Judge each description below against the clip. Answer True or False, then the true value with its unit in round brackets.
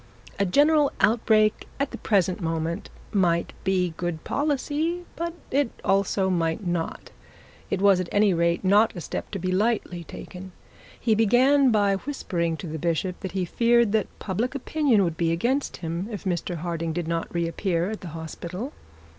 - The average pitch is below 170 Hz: False (190 Hz)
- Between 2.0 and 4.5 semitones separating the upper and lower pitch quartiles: False (5.2 semitones)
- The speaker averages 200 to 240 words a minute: False (170 wpm)